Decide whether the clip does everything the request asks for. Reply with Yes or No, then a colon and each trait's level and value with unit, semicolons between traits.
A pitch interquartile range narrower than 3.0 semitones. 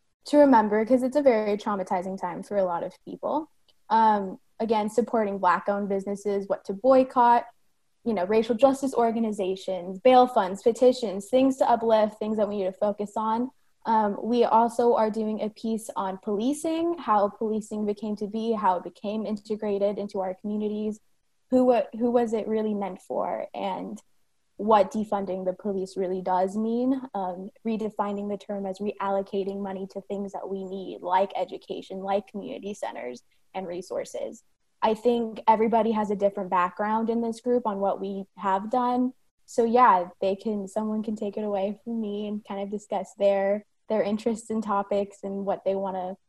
Yes: narrow, 2.5 semitones